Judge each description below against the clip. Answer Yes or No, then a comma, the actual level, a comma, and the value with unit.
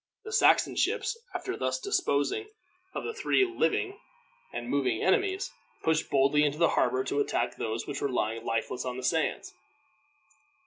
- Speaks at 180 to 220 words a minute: No, average, 160 wpm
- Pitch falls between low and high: Yes, medium, 145 Hz